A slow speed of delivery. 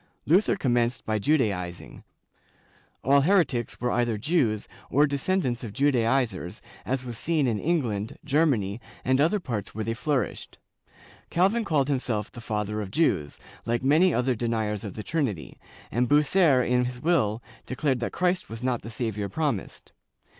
No: average, 155 wpm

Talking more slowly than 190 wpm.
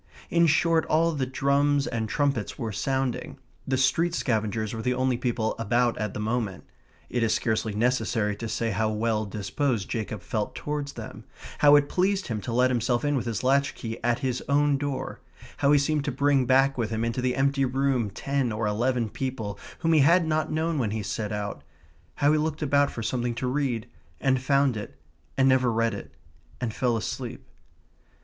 No: average, 195 wpm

